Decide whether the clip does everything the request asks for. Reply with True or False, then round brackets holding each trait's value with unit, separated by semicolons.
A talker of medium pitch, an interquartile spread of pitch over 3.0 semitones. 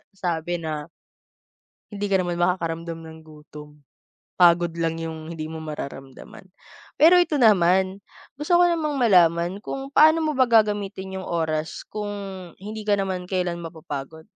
True (180 Hz; 4.3 semitones)